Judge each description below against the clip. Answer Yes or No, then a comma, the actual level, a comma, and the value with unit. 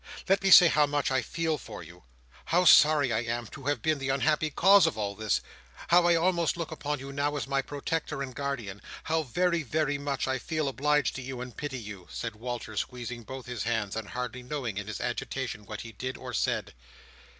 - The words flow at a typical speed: No, fast, 215 wpm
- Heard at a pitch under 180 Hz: Yes, low, 135 Hz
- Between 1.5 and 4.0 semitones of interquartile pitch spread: No, average, 4.5 semitones